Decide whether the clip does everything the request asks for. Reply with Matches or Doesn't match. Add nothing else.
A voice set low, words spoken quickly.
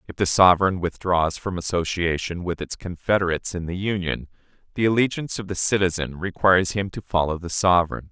Doesn't match